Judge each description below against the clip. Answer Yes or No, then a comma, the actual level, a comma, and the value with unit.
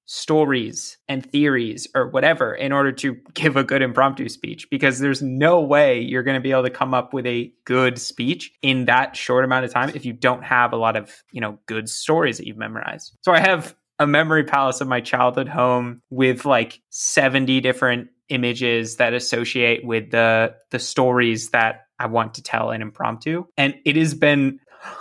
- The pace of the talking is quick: No, average, 195 wpm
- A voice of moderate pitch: No, low, 130 Hz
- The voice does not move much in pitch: Yes, narrow, 2.1 semitones